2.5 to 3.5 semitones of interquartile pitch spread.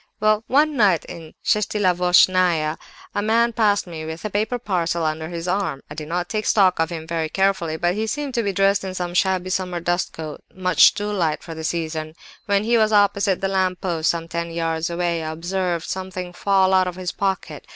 Yes: average, 3.2 semitones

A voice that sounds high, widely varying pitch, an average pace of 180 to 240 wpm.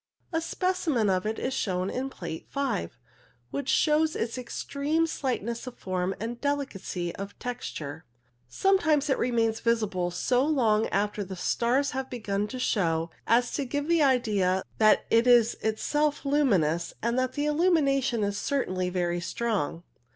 No: high, 235 Hz; wide, 6.4 semitones; average, 150 wpm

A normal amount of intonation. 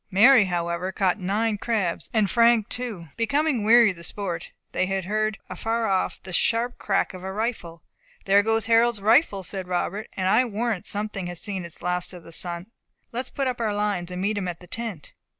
Yes: average, 3.9 semitones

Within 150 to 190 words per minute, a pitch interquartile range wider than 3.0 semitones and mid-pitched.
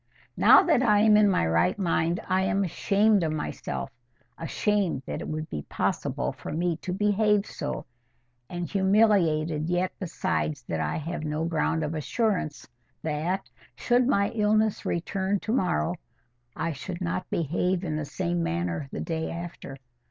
Yes: average, 160 wpm; average, 4.6 semitones; medium, 175 Hz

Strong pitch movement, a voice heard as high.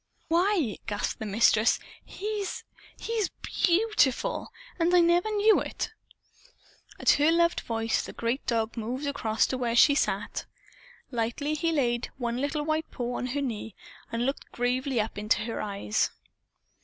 Yes: wide, 6.4 semitones; very high, 260 Hz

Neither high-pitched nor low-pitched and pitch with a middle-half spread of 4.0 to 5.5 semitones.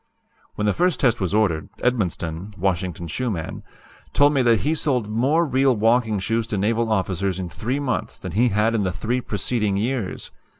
No: low, 110 Hz; average, 4.4 semitones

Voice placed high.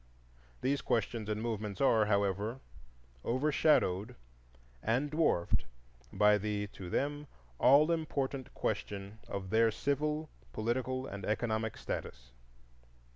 No: low, 115 Hz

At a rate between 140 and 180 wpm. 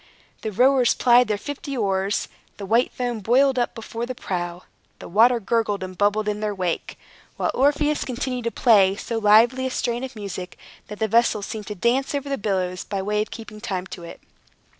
No: average, 200 wpm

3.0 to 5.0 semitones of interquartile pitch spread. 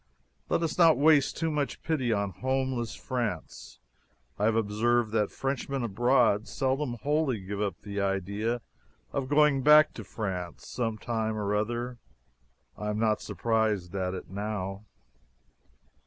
Yes: average, 4.4 semitones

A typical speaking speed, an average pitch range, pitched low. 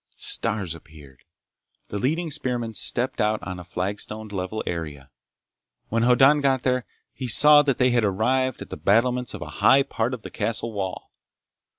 Yes: average, 170 wpm; average, 4.9 semitones; low, 115 Hz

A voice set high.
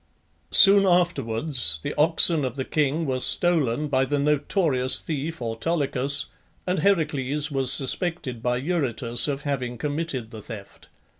No: medium, 140 Hz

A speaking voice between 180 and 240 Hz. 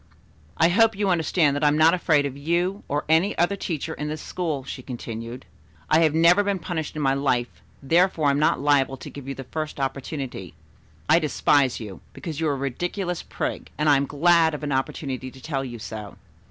No: medium, 150 Hz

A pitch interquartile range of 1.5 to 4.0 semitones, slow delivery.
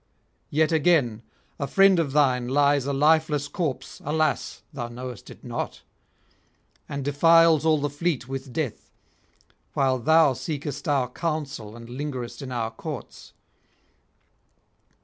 Yes: average, 3.5 semitones; slow, 130 wpm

